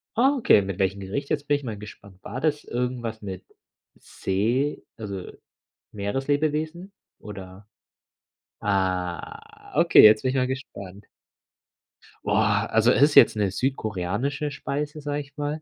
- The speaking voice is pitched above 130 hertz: No, low, 120 Hz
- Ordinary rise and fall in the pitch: No, wide, 6.4 semitones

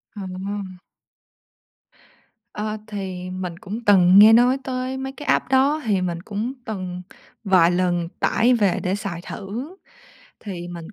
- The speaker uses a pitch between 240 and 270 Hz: No, high, 200 Hz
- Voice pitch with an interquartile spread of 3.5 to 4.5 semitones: Yes, average, 3.8 semitones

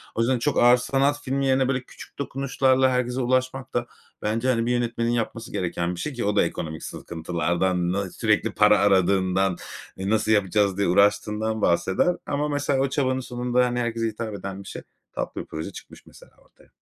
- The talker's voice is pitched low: Yes, low, 115 Hz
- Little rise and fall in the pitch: No, average, 4.7 semitones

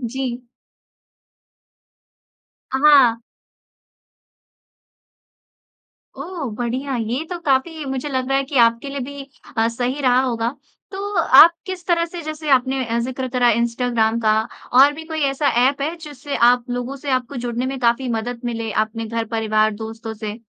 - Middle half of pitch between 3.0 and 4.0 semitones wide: Yes, average, 3.5 semitones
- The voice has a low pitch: No, very high, 255 Hz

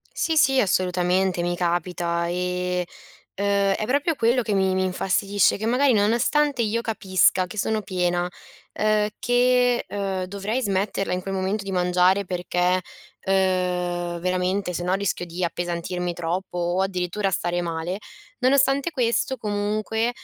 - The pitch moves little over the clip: No, average, 3.1 semitones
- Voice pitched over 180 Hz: Yes, high, 190 Hz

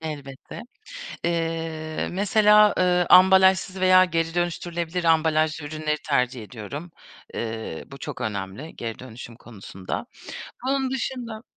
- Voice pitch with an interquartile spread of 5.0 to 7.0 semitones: Yes, wide, 5.6 semitones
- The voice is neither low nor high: Yes, medium, 165 Hz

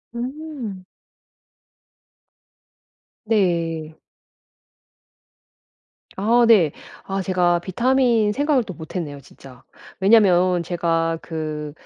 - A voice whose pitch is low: No, medium, 185 Hz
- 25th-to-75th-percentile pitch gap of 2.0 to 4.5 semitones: No, wide, 5.5 semitones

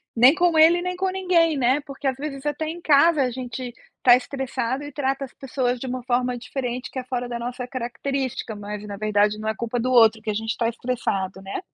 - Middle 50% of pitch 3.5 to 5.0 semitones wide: No, average, 2.9 semitones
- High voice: Yes, very high, 255 Hz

